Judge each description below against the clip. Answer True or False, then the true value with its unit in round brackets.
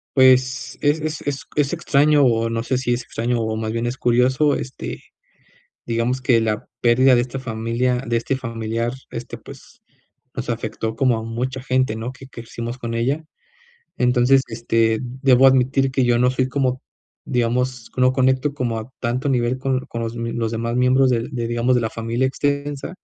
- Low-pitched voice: True (125 Hz)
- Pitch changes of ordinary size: False (2.1 semitones)